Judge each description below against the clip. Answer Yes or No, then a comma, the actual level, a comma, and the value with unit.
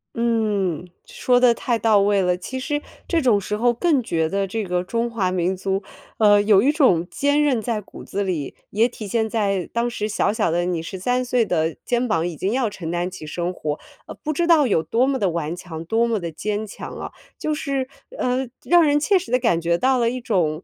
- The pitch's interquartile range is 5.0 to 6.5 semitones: Yes, wide, 5.6 semitones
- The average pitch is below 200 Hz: No, high, 210 Hz